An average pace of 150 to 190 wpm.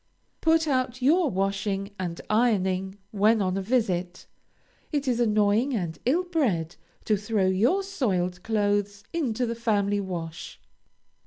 No: slow, 135 wpm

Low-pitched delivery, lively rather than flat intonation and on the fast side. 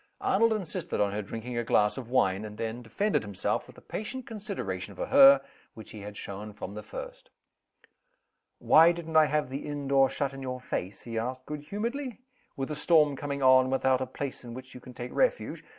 Yes: low, 130 Hz; wide, 6.4 semitones; fast, 215 wpm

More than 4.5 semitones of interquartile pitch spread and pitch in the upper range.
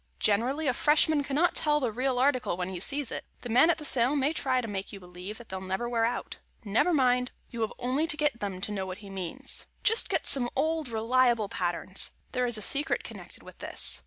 Yes: wide, 5.6 semitones; high, 245 Hz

